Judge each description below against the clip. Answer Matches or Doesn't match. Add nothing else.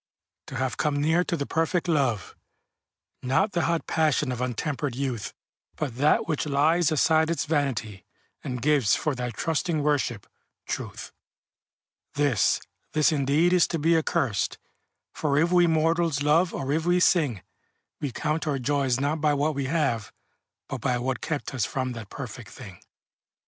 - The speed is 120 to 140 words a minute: Doesn't match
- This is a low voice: Doesn't match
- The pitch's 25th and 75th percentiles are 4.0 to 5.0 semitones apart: Doesn't match